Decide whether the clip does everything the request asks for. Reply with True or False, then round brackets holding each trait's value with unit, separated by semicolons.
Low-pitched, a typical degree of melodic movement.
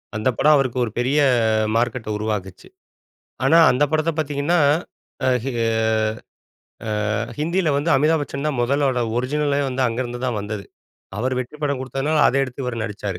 True (130 Hz; 3.5 semitones)